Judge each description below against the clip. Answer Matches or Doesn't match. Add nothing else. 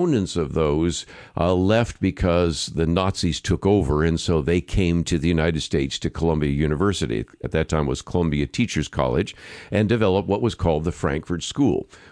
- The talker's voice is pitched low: Matches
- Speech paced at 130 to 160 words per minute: Doesn't match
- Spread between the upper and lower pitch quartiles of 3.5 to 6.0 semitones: Doesn't match